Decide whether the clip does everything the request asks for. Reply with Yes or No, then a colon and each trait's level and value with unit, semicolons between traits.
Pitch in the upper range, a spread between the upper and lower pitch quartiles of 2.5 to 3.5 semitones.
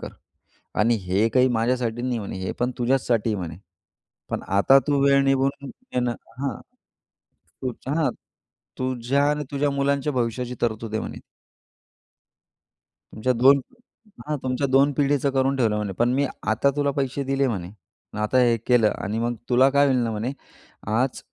No: low, 125 Hz; average, 3.2 semitones